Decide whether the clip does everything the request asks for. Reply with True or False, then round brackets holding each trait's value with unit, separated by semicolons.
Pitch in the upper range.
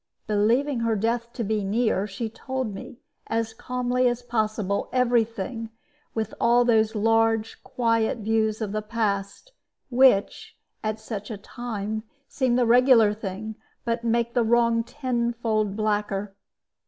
True (225 Hz)